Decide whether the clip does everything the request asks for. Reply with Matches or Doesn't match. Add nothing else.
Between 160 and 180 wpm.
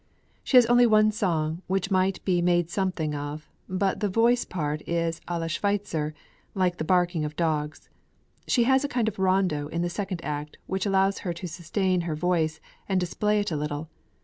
Doesn't match